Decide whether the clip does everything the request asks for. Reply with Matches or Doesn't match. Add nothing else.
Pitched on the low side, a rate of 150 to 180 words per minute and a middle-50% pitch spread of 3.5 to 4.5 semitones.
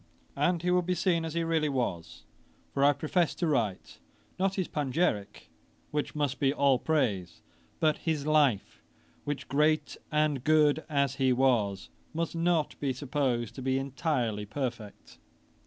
Doesn't match